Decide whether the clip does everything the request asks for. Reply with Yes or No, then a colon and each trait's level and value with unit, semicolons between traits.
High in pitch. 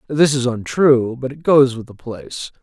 No: low, 130 Hz